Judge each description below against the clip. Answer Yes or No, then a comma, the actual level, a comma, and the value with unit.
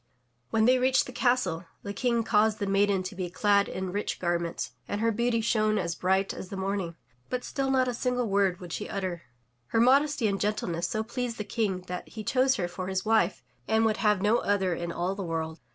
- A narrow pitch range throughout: No, average, 3.8 semitones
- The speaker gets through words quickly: Yes, fast, 220 wpm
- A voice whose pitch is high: Yes, high, 205 Hz